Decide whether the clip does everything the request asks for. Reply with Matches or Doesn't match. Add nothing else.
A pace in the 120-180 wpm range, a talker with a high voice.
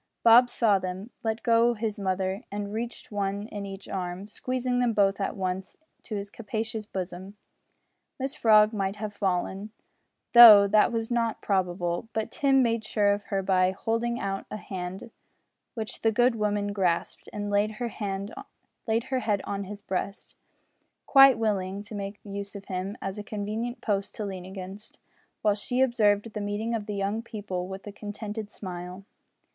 Matches